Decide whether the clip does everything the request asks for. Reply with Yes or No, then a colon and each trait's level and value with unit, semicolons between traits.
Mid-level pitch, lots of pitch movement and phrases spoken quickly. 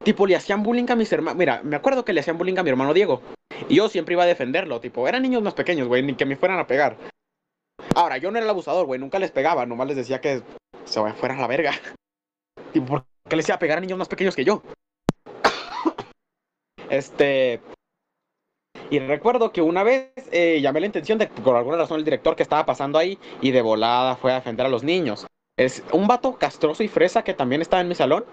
Yes: medium, 175 Hz; wide, 7.7 semitones; fast, 230 wpm